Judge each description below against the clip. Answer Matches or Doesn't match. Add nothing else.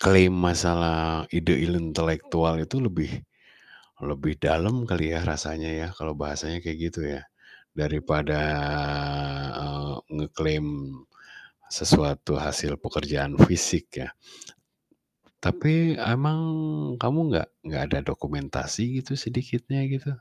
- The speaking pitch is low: Matches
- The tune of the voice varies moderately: Doesn't match